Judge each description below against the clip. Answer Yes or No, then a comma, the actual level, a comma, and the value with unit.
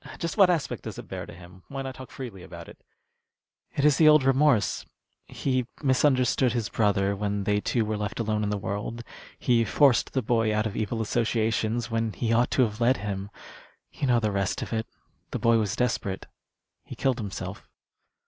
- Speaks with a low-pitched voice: Yes, low, 115 Hz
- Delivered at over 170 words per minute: Yes, average, 195 wpm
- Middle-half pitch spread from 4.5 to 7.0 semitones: No, average, 3.7 semitones